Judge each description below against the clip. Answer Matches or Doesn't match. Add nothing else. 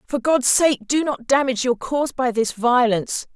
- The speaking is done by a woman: Matches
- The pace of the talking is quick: Doesn't match